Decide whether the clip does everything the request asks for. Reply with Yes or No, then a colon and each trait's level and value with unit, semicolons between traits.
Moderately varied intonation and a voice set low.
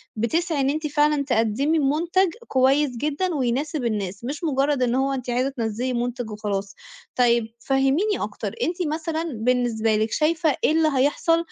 No: average, 4.5 semitones; very high, 270 Hz